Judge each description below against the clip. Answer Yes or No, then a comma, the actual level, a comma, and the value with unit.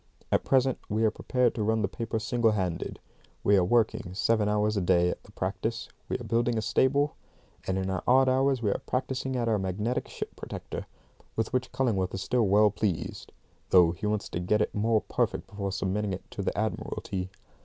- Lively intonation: No, average, 3.8 semitones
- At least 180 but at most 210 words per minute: Yes, fast, 205 wpm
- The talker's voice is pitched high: No, low, 105 Hz